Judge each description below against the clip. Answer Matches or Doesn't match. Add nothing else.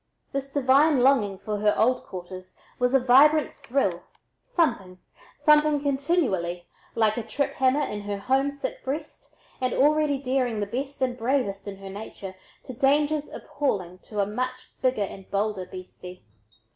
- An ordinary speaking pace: Matches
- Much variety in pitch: Matches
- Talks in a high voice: Matches